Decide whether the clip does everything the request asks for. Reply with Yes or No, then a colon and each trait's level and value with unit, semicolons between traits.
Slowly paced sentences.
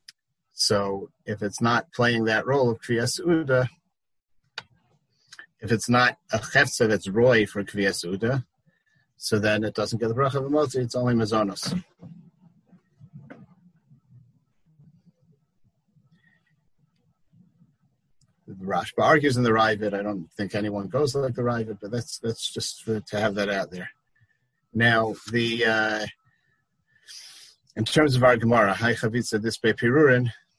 Yes: slow, 125 wpm